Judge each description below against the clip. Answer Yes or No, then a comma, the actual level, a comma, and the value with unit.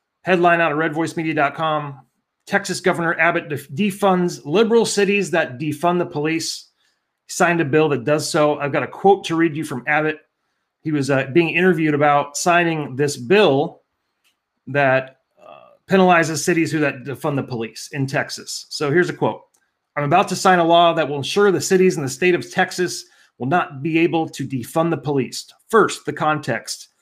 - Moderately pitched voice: Yes, medium, 160 Hz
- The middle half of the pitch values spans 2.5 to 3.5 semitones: Yes, average, 3.2 semitones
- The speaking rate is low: No, average, 180 wpm